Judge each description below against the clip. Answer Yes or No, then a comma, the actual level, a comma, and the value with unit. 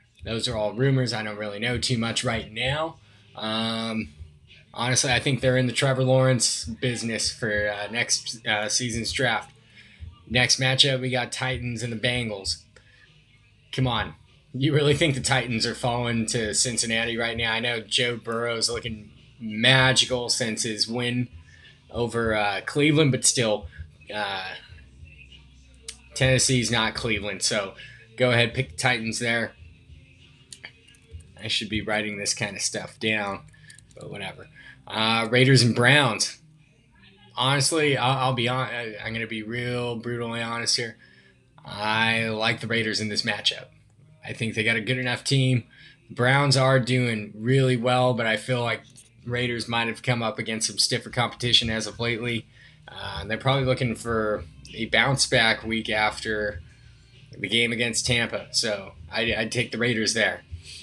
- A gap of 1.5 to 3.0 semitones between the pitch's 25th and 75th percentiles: Yes, narrow, 2.6 semitones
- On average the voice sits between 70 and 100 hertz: No, low, 115 Hz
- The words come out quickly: No, average, 155 wpm